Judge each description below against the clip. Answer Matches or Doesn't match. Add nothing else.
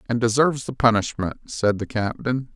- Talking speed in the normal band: Matches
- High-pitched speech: Doesn't match